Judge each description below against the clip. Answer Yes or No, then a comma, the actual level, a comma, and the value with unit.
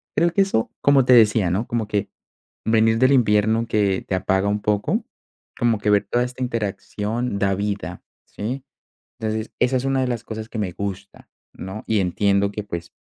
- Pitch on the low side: Yes, low, 110 Hz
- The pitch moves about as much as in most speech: Yes, average, 3.0 semitones